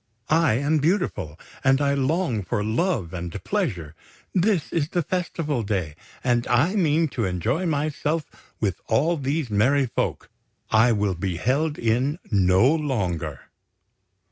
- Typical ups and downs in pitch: No, wide, 7.4 semitones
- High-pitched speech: No, low, 130 Hz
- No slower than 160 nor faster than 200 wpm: No, average, 140 wpm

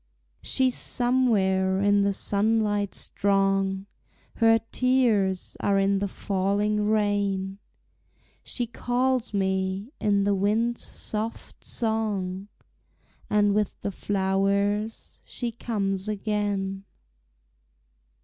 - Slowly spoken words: Yes, slow, 90 wpm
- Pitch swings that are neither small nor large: No, narrow, 2.0 semitones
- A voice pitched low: No, high, 205 Hz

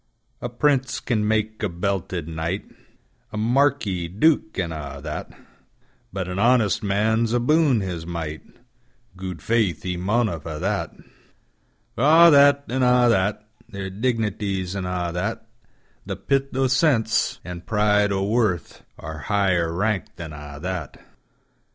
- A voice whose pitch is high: No, low, 100 Hz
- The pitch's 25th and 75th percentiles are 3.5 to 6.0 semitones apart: Yes, average, 4.9 semitones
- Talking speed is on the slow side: Yes, slow, 120 wpm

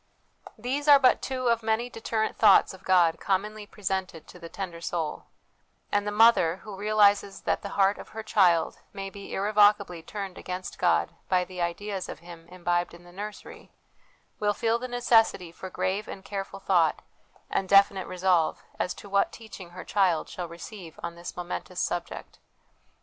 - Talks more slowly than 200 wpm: Yes, average, 170 wpm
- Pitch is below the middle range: No, high, 195 Hz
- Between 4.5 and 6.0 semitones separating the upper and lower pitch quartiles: No, average, 3.1 semitones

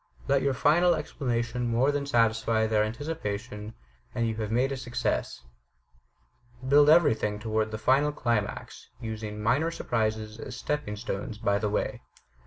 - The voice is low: Yes, low, 115 Hz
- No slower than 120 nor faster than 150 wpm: Yes, average, 145 wpm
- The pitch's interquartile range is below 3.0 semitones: No, average, 4.3 semitones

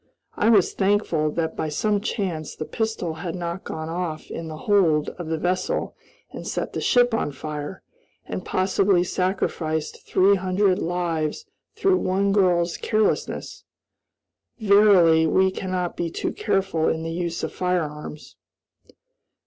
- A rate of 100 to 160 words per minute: Yes, average, 140 wpm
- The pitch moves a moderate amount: Yes, average, 3.5 semitones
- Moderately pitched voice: Yes, medium, 180 Hz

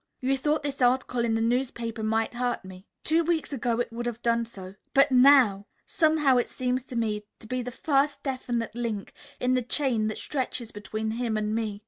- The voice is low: No, high, 240 Hz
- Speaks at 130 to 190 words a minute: No, average, 200 wpm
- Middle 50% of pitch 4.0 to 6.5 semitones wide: No, average, 2.9 semitones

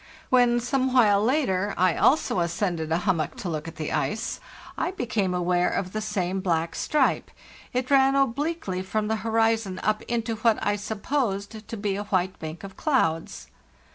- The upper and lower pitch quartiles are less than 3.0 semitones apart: No, average, 4.6 semitones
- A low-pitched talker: No, high, 205 Hz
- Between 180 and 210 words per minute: No, average, 170 wpm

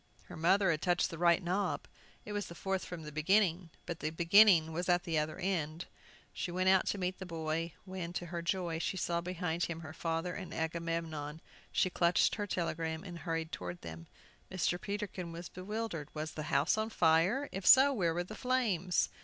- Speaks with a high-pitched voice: No, medium, 175 Hz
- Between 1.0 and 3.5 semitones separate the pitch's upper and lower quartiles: Yes, narrow, 2.6 semitones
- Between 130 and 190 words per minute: No, average, 200 wpm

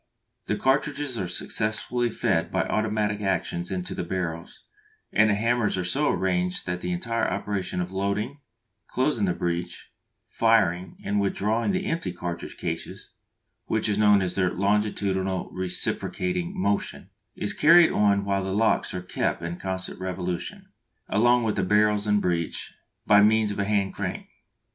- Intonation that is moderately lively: Yes, average, 3.1 semitones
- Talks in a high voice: No, low, 100 Hz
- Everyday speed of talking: Yes, average, 155 wpm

